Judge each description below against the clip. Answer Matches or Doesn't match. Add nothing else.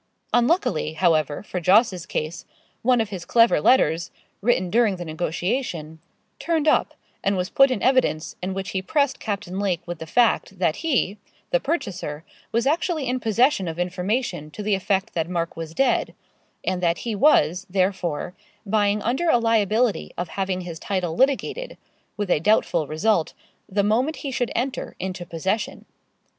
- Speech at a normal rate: Matches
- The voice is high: Matches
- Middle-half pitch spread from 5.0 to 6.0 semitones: Matches